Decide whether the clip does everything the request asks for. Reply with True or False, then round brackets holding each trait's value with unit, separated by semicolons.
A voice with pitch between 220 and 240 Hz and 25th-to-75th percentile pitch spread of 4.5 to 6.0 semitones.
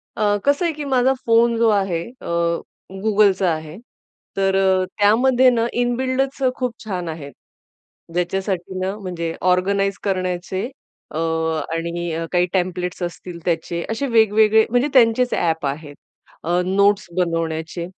False (190 Hz; 4.8 semitones)